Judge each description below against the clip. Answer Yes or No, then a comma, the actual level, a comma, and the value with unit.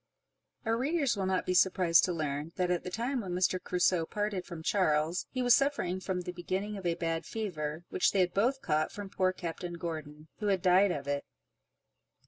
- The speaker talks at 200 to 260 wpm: Yes, fast, 205 wpm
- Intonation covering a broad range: No, average, 3.3 semitones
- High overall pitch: No, medium, 180 Hz